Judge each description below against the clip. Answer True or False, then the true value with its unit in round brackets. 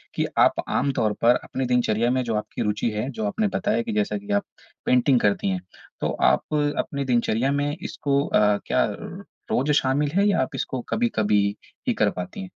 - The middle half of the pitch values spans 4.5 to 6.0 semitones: True (5.1 semitones)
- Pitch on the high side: False (130 Hz)